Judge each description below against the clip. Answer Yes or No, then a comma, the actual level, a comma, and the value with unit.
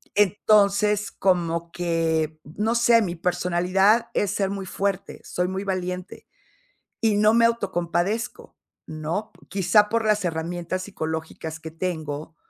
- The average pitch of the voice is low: No, medium, 185 Hz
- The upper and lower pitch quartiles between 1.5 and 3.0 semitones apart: No, average, 3.7 semitones